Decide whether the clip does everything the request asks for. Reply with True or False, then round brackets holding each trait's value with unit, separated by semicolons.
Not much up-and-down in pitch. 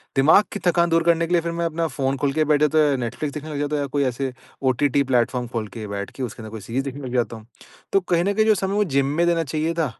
False (4.4 semitones)